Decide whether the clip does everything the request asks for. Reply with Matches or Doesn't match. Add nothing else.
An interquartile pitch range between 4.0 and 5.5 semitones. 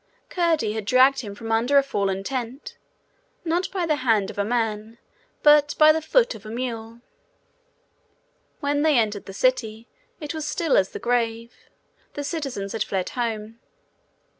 Matches